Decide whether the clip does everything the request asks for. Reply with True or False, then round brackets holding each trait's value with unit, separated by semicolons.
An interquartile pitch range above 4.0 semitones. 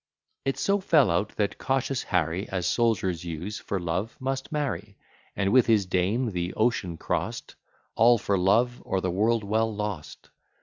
True (4.7 semitones)